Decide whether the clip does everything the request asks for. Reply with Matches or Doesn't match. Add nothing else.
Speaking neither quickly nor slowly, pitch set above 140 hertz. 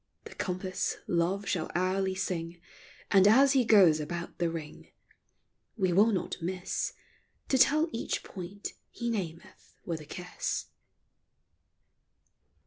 Doesn't match